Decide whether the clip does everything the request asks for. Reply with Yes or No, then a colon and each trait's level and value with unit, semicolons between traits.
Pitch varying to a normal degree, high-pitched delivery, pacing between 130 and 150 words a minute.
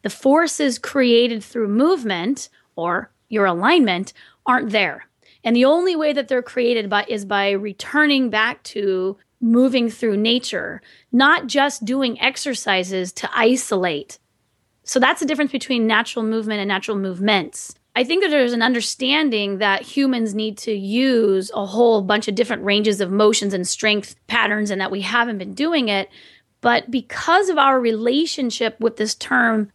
No: average, 4.1 semitones; high, 230 Hz; average, 160 wpm